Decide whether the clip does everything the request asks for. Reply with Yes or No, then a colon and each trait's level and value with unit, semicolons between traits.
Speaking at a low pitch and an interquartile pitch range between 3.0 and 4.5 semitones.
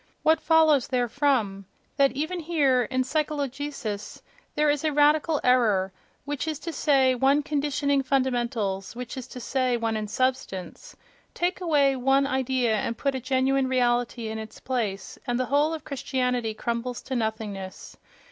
No: very high, 260 Hz; average, 3.4 semitones